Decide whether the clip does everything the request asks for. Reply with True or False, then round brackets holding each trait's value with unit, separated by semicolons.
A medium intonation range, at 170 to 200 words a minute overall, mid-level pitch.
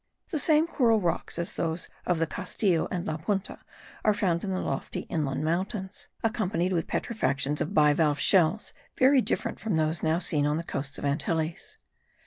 True (4.5 semitones; 180 wpm; 170 Hz)